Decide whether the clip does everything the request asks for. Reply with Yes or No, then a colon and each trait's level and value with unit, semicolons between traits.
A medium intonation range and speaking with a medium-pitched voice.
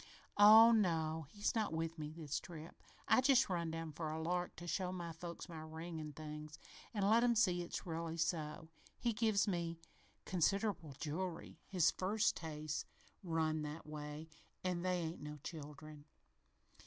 Yes: average, 3.0 semitones; medium, 165 Hz